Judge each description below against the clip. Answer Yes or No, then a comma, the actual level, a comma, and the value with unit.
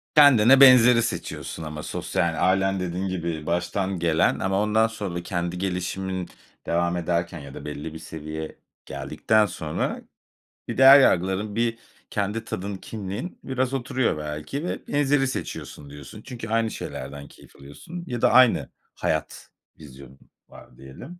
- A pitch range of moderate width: No, wide, 5.7 semitones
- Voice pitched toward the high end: No, very low, 95 Hz